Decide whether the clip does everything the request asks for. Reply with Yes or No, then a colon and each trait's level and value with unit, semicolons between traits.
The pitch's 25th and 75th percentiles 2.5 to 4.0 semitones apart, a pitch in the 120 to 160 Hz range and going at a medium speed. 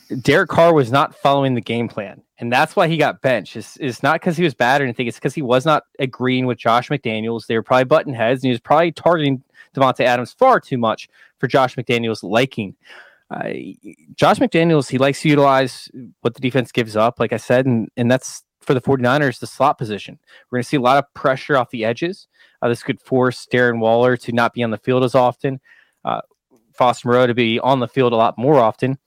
No: average, 2.8 semitones; low, 130 Hz; fast, 230 wpm